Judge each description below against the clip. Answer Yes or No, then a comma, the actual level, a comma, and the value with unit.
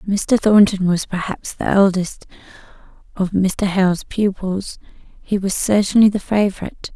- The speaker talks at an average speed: No, slow, 130 wpm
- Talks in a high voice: Yes, high, 195 Hz